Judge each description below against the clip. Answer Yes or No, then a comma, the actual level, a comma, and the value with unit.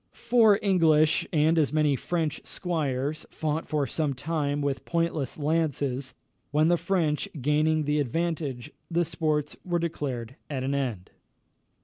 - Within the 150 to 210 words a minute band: No, slow, 135 wpm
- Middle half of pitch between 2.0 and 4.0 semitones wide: Yes, average, 2.8 semitones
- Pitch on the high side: No, medium, 150 Hz